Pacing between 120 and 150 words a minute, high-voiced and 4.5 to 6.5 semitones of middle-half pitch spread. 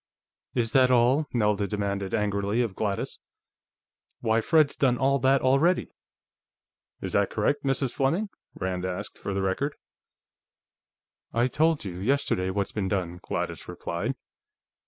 No: slow, 135 wpm; low, 115 Hz; wide, 5.4 semitones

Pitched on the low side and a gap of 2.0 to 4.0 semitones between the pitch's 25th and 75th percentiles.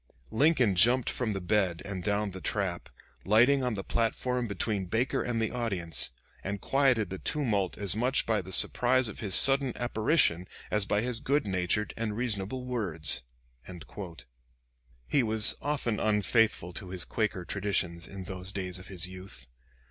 No: low, 105 Hz; average, 4.4 semitones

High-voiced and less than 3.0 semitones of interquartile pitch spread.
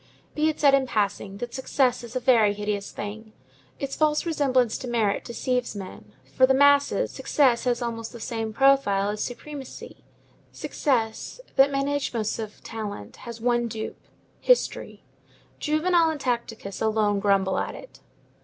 No: high, 240 Hz; average, 4.3 semitones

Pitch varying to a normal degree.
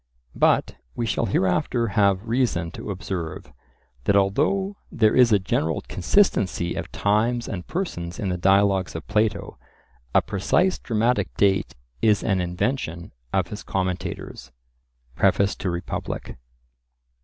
Yes: average, 4.3 semitones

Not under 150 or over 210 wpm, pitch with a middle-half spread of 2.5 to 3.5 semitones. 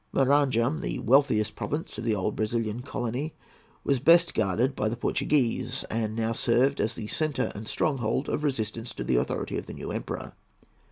No: average, 175 wpm; average, 4.2 semitones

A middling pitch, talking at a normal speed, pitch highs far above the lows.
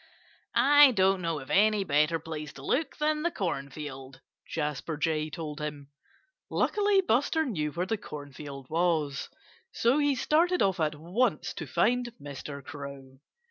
Yes: medium, 160 Hz; average, 145 wpm; wide, 8.6 semitones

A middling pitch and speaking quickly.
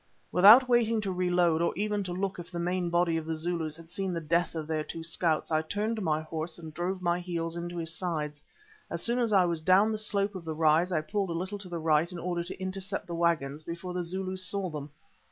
Yes: medium, 175 Hz; fast, 245 wpm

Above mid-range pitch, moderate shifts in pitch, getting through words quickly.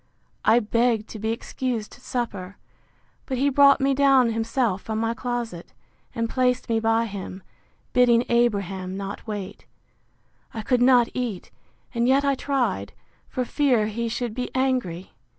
No: high, 235 Hz; average, 3.0 semitones; average, 150 wpm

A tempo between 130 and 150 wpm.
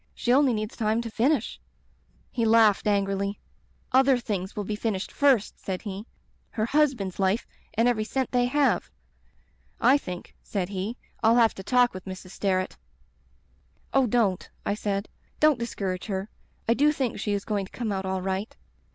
No: average, 175 wpm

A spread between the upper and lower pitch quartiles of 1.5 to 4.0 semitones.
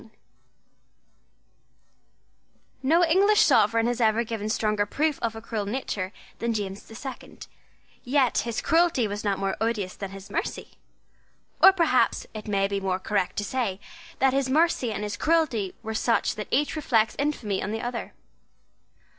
No: average, 4.6 semitones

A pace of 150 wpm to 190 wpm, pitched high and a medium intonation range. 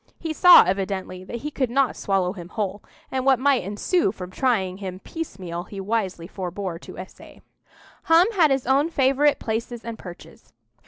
No: average, 170 wpm; high, 220 Hz; wide, 6.4 semitones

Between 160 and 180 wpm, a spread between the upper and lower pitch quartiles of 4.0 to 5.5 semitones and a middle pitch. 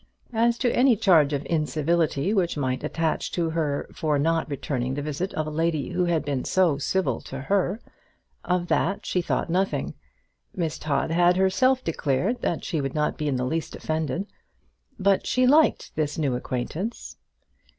Yes: average, 170 wpm; average, 4.5 semitones; medium, 165 Hz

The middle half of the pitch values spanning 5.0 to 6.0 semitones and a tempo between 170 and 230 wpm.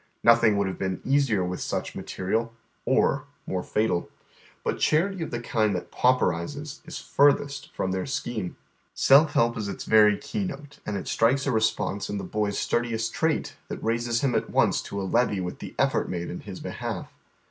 Yes: average, 5.3 semitones; average, 195 wpm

